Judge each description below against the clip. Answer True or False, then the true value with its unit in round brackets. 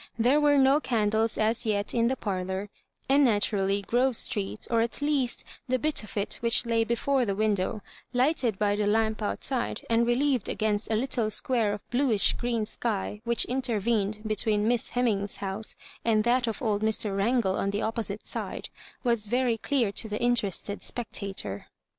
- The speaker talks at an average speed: True (175 wpm)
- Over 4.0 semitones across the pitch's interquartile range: False (2.9 semitones)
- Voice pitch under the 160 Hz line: False (225 Hz)